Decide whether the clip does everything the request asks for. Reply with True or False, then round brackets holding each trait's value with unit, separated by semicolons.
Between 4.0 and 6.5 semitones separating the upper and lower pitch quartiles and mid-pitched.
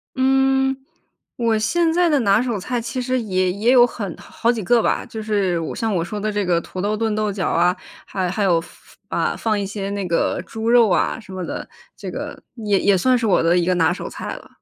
False (4.3 semitones; 210 Hz)